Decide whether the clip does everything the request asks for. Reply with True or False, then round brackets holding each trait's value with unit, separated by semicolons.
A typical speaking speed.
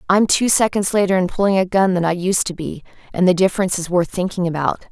False (245 wpm)